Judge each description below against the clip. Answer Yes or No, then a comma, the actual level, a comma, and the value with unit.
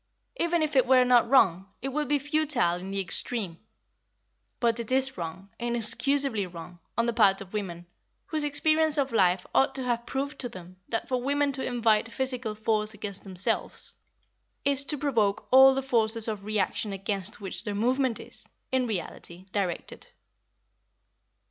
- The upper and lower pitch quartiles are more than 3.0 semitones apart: Yes, average, 5.2 semitones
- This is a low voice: No, high, 230 Hz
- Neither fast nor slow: Yes, average, 165 wpm